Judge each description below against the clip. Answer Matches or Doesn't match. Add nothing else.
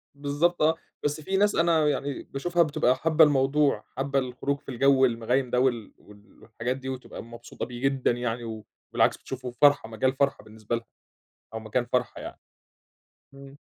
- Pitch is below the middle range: Matches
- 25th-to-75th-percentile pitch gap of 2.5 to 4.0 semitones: Matches